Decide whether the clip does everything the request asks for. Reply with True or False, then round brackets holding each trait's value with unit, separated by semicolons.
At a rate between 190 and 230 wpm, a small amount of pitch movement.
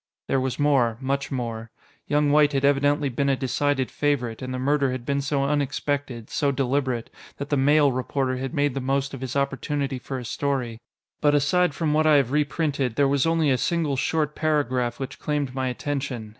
True (200 wpm; 2.0 semitones)